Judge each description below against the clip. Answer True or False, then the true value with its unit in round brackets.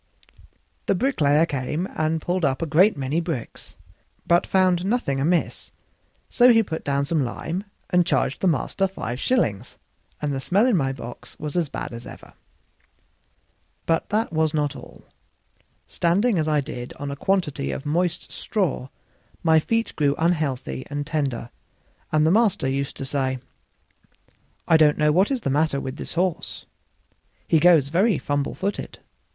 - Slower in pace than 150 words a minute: False (160 wpm)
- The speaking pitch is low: False (155 Hz)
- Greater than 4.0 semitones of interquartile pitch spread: True (4.5 semitones)